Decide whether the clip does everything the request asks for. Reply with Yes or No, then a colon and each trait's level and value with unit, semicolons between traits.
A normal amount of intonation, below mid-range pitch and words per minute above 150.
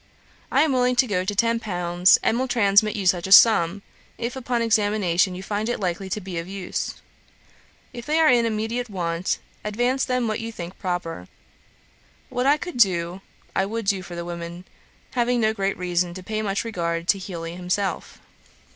No: average, 4.5 semitones; high, 200 Hz; average, 190 wpm